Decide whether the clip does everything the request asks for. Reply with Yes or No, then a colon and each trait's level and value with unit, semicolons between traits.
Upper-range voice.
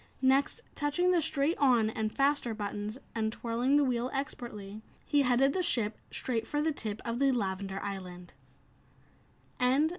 Yes: high, 240 Hz